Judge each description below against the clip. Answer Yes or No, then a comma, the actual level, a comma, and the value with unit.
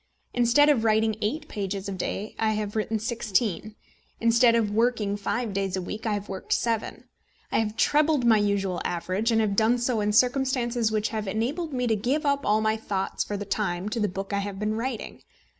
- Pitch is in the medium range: No, high, 220 Hz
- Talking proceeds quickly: Yes, fast, 210 wpm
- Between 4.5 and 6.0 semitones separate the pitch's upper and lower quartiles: No, average, 2.7 semitones